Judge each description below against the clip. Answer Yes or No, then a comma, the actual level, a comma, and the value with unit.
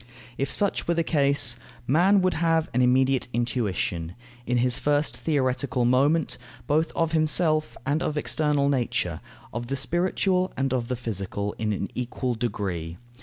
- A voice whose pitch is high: No, low, 135 Hz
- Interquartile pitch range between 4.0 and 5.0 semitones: Yes, average, 4.7 semitones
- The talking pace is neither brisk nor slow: Yes, average, 155 wpm